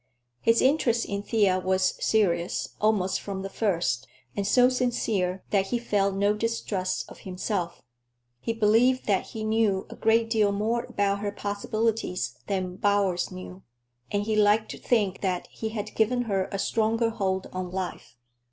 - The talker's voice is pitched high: Yes, high, 205 Hz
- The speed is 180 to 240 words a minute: No, average, 160 wpm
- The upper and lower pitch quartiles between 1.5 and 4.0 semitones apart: Yes, average, 2.9 semitones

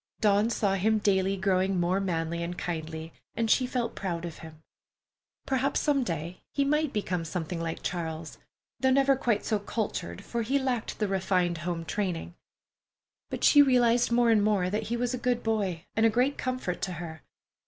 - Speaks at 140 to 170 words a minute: No, average, 185 wpm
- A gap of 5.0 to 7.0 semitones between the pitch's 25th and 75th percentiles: Yes, wide, 5.5 semitones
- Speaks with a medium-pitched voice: No, high, 200 Hz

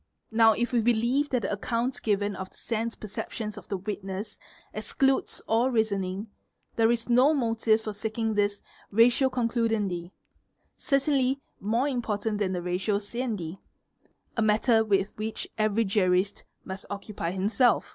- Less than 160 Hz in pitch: No, high, 220 Hz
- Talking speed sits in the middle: Yes, average, 145 wpm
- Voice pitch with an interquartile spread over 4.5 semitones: No, average, 2.7 semitones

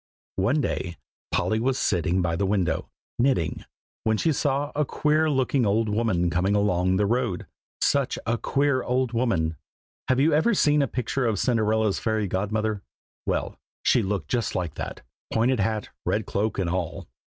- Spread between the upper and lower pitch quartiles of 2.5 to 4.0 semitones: No, wide, 5.4 semitones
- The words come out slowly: No, average, 165 wpm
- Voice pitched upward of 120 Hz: No, low, 110 Hz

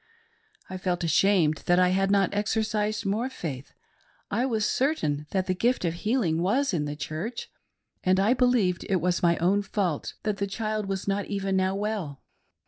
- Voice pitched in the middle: No, high, 195 Hz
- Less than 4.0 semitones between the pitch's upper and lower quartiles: Yes, average, 3.3 semitones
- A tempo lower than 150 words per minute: No, average, 180 wpm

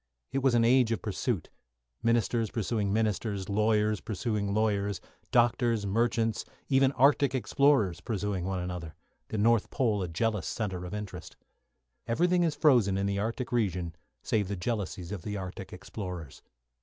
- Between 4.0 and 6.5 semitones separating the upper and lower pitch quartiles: No, average, 3.5 semitones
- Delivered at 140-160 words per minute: Yes, average, 150 wpm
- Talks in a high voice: No, low, 105 Hz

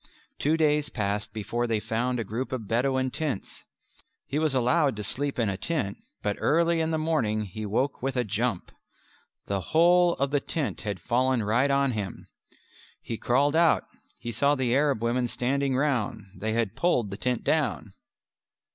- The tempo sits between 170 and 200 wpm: Yes, average, 175 wpm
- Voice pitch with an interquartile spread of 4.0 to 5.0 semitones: Yes, average, 4.7 semitones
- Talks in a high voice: No, low, 125 Hz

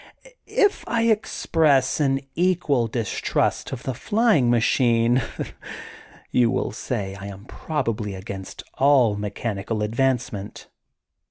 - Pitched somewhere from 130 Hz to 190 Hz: No, low, 120 Hz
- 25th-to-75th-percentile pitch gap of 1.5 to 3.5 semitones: No, average, 4.9 semitones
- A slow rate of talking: Yes, slow, 105 wpm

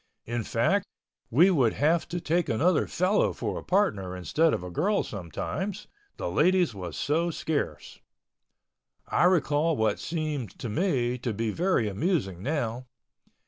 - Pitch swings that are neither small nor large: No, wide, 7.9 semitones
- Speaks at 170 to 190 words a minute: No, average, 145 wpm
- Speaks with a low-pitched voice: No, medium, 150 Hz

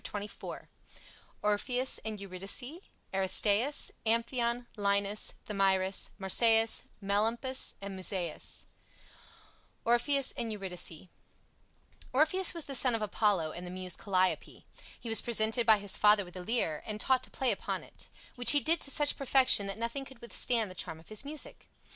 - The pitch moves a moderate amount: Yes, average, 4.2 semitones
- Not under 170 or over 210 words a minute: No, average, 150 wpm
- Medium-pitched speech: No, high, 220 Hz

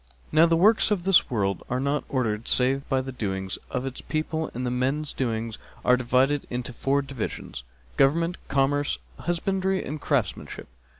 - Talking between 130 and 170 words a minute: Yes, average, 160 wpm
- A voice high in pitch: No, low, 135 Hz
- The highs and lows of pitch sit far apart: No, average, 3.8 semitones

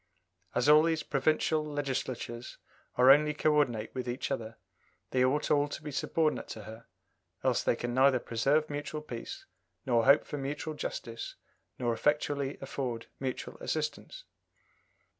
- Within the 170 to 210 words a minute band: No, average, 145 wpm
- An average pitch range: Yes, average, 3.6 semitones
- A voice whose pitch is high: No, medium, 140 Hz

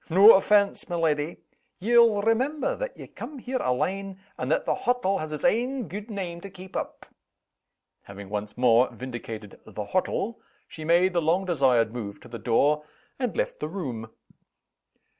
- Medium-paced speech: Yes, average, 165 wpm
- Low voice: No, medium, 175 Hz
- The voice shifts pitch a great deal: Yes, wide, 8.9 semitones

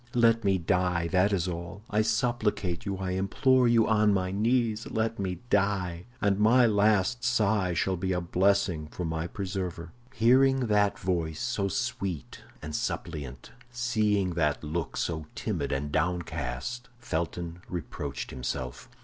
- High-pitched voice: No, very low, 95 Hz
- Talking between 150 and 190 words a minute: No, average, 140 wpm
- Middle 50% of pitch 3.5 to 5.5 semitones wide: Yes, average, 4.2 semitones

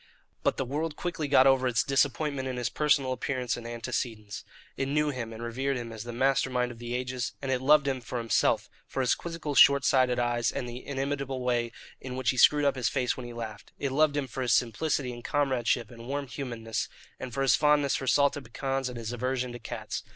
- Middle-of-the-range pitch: No, low, 130 Hz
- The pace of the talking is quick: Yes, fast, 225 wpm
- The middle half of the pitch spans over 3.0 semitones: No, narrow, 2.5 semitones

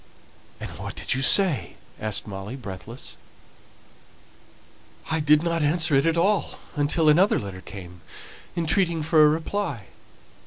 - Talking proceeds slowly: Yes, slow, 130 wpm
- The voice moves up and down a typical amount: No, wide, 7.4 semitones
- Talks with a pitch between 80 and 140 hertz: No, medium, 150 Hz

